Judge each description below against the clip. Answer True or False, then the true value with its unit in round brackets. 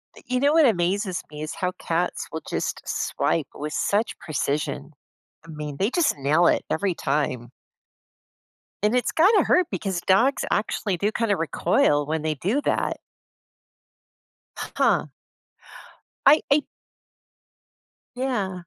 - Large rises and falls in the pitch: True (7.9 semitones)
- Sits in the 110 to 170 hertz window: False (185 Hz)